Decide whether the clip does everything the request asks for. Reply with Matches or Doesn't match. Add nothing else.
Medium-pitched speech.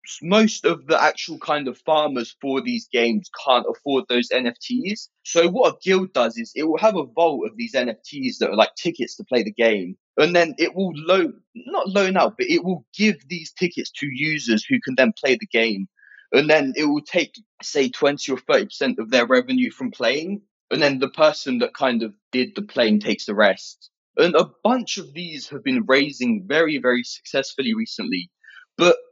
Matches